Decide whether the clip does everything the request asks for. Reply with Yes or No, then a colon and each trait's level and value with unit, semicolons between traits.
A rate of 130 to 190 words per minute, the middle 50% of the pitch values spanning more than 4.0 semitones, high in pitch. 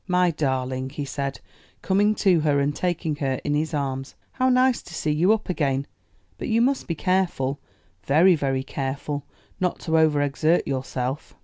No: average, 170 wpm; average, 4.7 semitones; medium, 150 Hz